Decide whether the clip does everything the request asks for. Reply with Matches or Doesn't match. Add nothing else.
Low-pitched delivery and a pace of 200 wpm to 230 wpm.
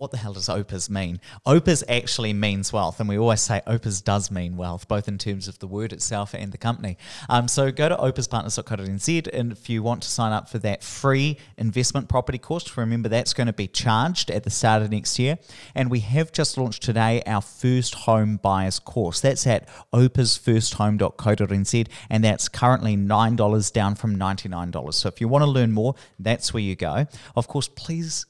Matches